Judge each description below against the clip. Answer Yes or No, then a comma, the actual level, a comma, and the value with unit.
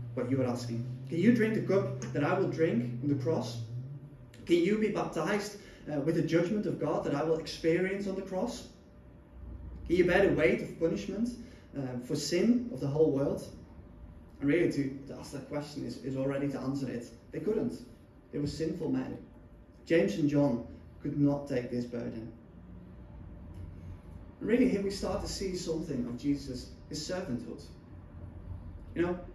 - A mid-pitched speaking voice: Yes, medium, 145 Hz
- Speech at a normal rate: Yes, average, 180 wpm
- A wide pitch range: Yes, wide, 6.3 semitones